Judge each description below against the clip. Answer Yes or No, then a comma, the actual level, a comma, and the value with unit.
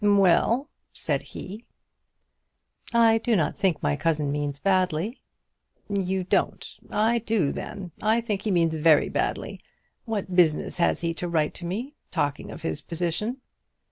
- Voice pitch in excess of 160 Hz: Yes, medium, 185 Hz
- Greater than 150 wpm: No, average, 145 wpm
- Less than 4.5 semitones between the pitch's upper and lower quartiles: No, average, 4.8 semitones